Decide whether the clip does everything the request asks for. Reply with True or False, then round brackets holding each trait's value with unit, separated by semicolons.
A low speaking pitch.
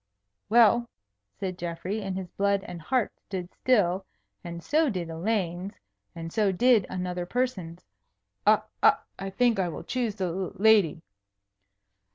False (190 Hz)